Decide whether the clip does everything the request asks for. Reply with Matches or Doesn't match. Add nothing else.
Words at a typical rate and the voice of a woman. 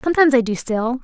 Doesn't match